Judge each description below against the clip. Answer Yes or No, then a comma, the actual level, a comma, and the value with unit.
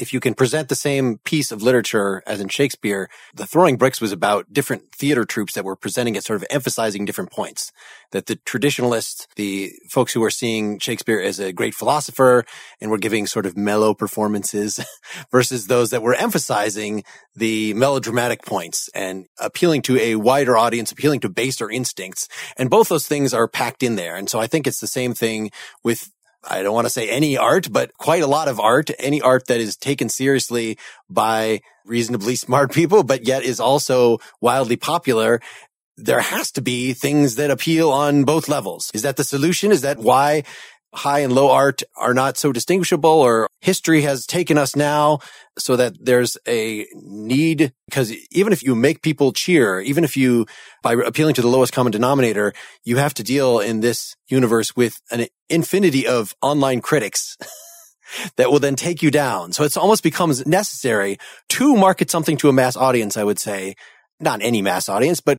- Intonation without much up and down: No, average, 4.5 semitones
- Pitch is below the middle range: Yes, low, 130 Hz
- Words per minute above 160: Yes, average, 190 wpm